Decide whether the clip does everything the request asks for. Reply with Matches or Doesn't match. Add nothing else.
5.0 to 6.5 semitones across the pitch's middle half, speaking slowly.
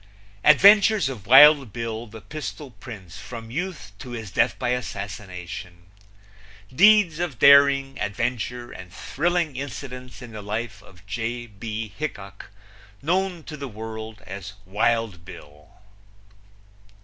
Matches